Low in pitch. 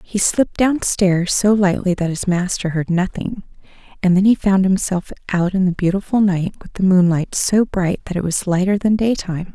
No: high, 190 Hz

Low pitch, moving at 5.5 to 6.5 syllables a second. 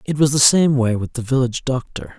Yes: low, 130 Hz; 5.7 syllables/s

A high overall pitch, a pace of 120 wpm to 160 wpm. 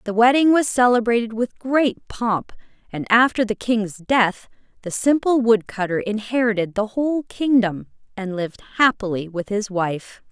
Yes: high, 225 Hz; average, 150 wpm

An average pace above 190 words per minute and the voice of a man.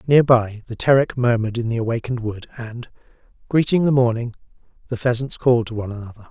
No: average, 180 wpm; male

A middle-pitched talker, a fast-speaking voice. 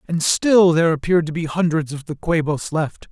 Yes: medium, 160 Hz; fast, 210 wpm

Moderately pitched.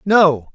Yes: medium, 165 Hz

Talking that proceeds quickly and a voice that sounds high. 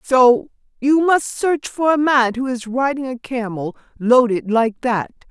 No: average, 170 wpm; very high, 250 Hz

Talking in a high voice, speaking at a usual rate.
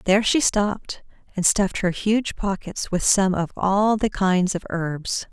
Yes: high, 195 Hz; average, 180 wpm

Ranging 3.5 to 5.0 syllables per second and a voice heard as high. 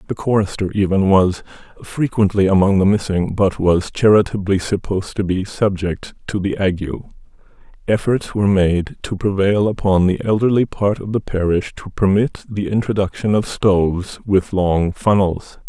No: 4.7 syllables/s; low, 100 Hz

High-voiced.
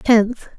Yes: high, 225 Hz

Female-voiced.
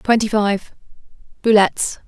Yes: female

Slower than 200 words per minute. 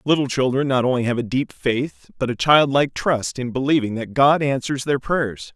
No: fast, 205 wpm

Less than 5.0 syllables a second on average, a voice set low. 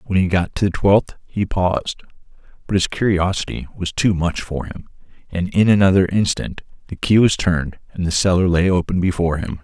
No: 5.5 syllables/s; very low, 90 Hz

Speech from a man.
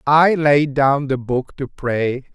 Yes: male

